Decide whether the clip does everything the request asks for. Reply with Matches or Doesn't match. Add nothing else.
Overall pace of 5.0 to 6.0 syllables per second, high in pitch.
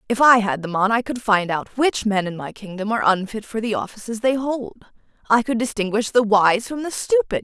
Matches